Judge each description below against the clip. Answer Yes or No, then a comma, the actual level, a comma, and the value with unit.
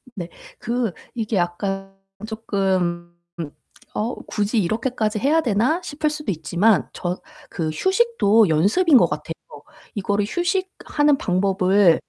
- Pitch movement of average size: No, wide, 6.1 semitones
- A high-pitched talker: Yes, high, 210 Hz